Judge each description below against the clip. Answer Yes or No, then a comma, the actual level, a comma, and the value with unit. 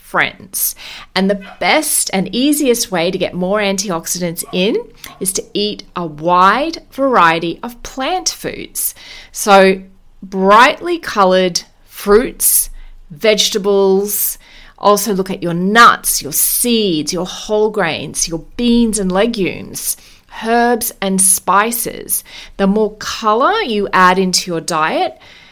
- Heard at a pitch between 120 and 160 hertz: No, high, 200 Hz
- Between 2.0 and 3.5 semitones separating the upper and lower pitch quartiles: Yes, average, 3.2 semitones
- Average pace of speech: No, slow, 120 wpm